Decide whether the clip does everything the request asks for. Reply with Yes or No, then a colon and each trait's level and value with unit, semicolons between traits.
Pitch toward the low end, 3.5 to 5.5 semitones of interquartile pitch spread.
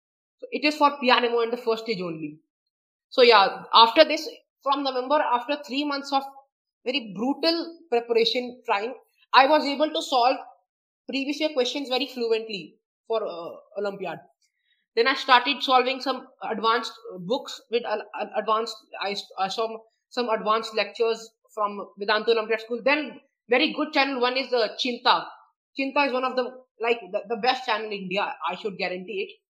No: very high, 250 Hz; average, 3.8 semitones